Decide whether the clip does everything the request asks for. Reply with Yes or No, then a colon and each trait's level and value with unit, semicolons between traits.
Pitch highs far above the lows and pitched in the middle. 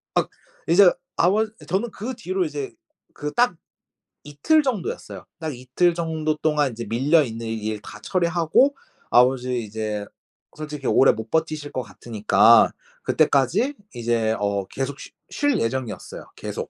Yes: wide, 7.1 semitones; medium, 145 Hz